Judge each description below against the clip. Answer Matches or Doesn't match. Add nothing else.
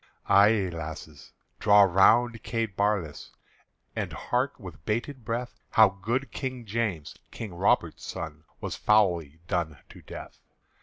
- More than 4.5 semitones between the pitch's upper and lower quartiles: Matches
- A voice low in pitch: Matches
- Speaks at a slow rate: Matches